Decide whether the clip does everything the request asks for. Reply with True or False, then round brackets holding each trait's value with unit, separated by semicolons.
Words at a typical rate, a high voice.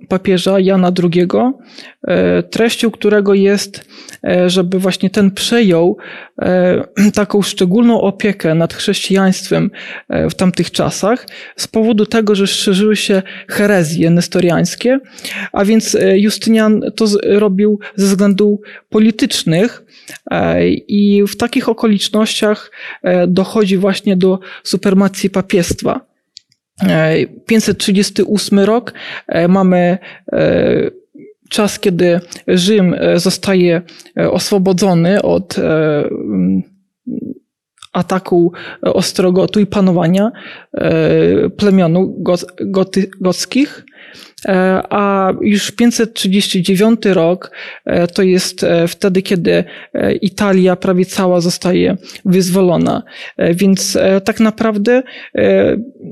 False (80 wpm; 195 Hz)